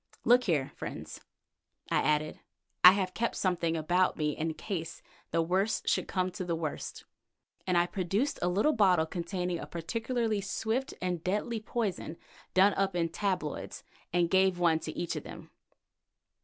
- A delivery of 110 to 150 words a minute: No, average, 160 wpm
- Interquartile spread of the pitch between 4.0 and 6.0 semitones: No, average, 3.3 semitones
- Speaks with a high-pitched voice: No, medium, 180 Hz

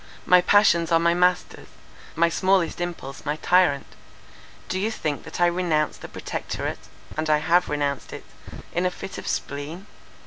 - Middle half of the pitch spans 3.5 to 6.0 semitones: No, average, 2.9 semitones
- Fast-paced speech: No, average, 165 wpm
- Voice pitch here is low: No, medium, 170 Hz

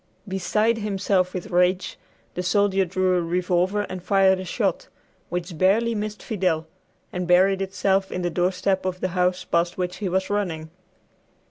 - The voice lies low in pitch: No, medium, 185 Hz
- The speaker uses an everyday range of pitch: No, narrow, 1.5 semitones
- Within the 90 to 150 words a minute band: No, average, 160 wpm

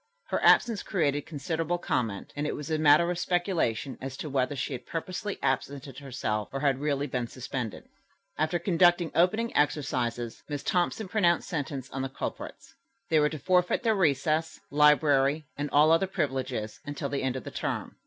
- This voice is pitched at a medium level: Yes, medium, 145 Hz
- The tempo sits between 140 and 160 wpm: No, average, 175 wpm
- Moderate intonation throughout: Yes, average, 4.3 semitones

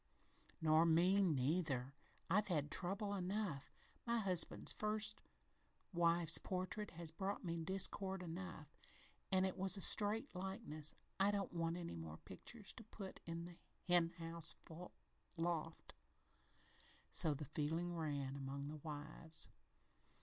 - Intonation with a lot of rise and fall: No, average, 3.7 semitones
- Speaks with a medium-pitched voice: Yes, medium, 170 Hz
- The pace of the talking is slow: Yes, slow, 130 wpm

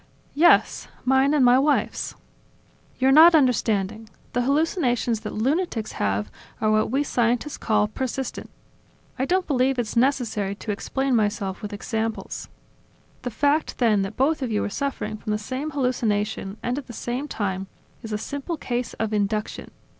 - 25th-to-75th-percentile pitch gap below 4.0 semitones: No, average, 4.3 semitones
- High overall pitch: Yes, high, 240 Hz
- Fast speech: No, average, 160 wpm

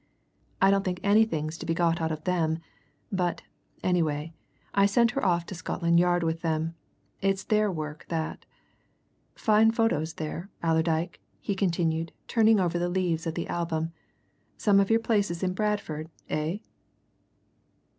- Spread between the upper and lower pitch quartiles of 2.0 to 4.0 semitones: Yes, average, 3.4 semitones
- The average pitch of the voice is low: No, medium, 175 Hz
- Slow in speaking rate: No, average, 150 wpm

